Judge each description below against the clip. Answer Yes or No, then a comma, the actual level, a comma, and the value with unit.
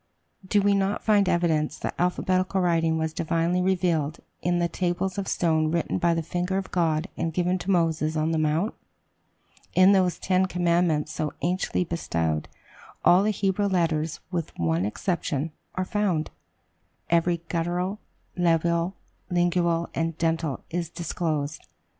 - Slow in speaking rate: No, average, 145 wpm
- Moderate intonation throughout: No, narrow, 2.3 semitones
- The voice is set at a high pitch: No, medium, 170 Hz